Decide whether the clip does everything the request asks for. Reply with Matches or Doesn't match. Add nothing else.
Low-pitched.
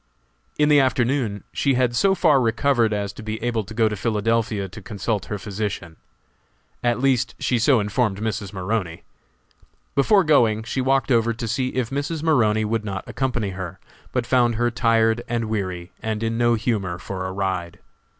Matches